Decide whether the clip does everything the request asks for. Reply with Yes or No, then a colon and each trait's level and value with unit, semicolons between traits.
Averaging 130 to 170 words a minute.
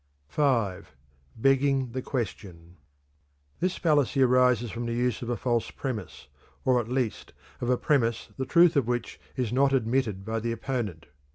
Yes: average, 160 wpm